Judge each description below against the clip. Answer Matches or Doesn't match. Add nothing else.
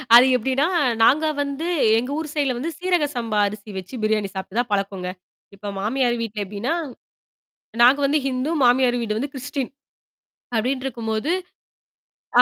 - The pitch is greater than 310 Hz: Doesn't match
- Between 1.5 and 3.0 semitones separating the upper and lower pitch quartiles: Doesn't match